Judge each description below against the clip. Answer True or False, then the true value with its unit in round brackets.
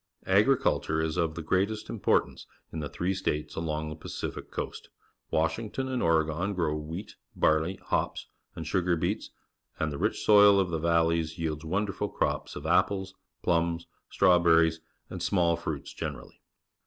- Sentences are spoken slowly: False (160 wpm)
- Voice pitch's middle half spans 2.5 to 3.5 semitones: True (2.9 semitones)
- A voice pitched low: True (85 Hz)